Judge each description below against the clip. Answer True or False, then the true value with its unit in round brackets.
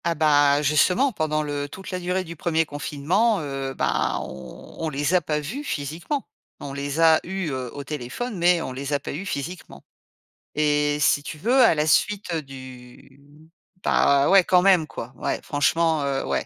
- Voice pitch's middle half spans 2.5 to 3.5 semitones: False (4.0 semitones)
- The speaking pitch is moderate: True (150 Hz)